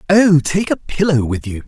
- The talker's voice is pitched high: No, medium, 150 Hz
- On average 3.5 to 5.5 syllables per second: Yes, 4.8 syllables/s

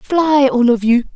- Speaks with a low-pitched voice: No, very high, 265 Hz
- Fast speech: Yes, fast, 210 wpm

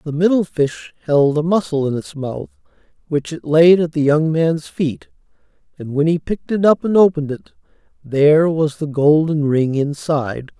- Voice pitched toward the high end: No, medium, 155 Hz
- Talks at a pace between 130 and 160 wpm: No, average, 180 wpm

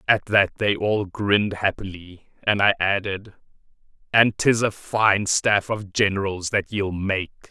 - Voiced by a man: Yes, male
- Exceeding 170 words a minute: No, average, 150 wpm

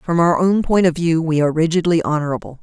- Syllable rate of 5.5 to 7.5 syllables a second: Yes, 6.5 syllables/s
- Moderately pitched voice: Yes, medium, 165 Hz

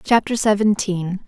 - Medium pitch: No, high, 205 Hz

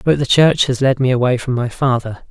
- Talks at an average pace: No, fast, 260 wpm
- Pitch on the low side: Yes, low, 130 Hz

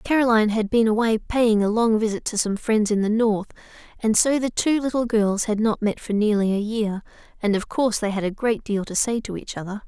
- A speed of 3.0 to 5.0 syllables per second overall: No, 5.5 syllables/s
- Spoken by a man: No, female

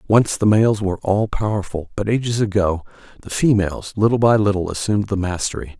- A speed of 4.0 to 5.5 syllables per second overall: No, 5.9 syllables/s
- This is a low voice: Yes, low, 100 Hz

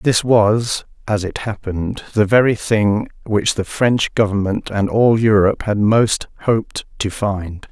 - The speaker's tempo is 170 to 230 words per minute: No, average, 155 wpm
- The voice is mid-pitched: No, low, 105 Hz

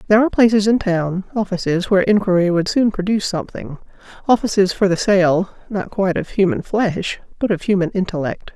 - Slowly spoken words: No, average, 155 wpm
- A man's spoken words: No, female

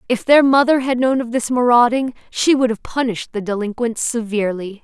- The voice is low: No, high, 240 Hz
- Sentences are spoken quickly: No, average, 185 wpm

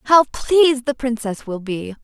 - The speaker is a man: No, female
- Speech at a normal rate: Yes, average, 175 wpm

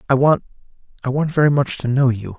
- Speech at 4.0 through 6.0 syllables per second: No, 6.3 syllables/s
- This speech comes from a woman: No, male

